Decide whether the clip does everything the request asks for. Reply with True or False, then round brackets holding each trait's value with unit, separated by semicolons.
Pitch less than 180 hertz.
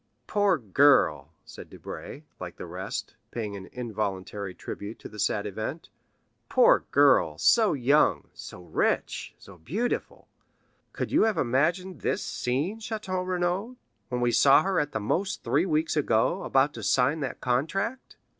True (140 Hz)